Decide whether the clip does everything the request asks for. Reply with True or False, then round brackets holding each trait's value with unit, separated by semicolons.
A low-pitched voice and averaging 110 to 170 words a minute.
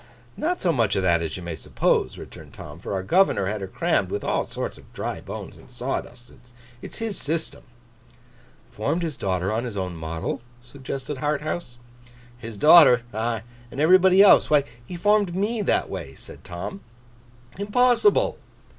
True (130 Hz; 165 wpm)